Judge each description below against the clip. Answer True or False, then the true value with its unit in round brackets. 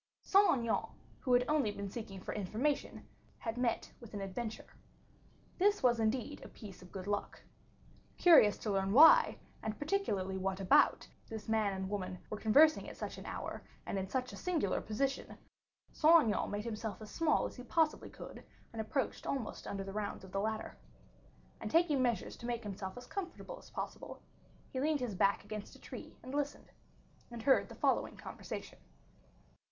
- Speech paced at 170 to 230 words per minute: True (180 wpm)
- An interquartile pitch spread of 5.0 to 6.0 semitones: True (5.5 semitones)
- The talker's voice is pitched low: False (225 Hz)